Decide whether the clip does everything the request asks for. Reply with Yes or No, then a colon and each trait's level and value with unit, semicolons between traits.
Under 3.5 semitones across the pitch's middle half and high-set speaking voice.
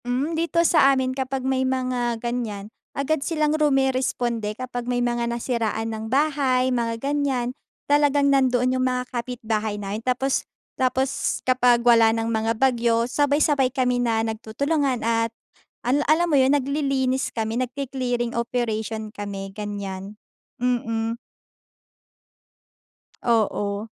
Yes: average, 2.9 semitones; high, 245 Hz